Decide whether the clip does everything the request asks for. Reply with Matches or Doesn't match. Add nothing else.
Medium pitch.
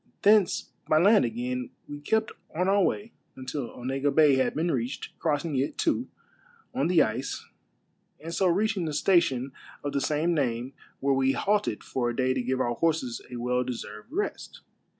Matches